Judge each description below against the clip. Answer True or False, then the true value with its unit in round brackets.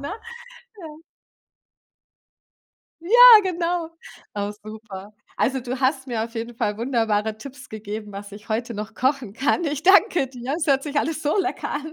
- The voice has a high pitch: True (255 Hz)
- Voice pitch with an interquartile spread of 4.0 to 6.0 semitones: True (5.5 semitones)